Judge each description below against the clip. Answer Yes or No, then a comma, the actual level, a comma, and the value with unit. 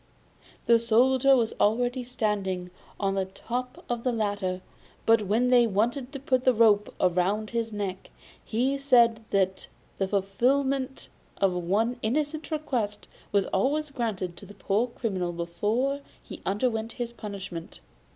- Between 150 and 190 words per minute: No, average, 140 wpm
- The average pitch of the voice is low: No, high, 225 Hz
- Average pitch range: Yes, average, 4.3 semitones